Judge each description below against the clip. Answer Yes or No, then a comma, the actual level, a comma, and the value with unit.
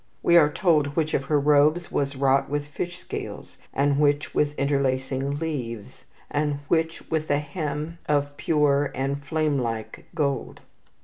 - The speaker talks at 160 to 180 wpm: No, average, 150 wpm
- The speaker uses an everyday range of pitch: No, narrow, 1.7 semitones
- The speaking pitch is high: No, medium, 145 Hz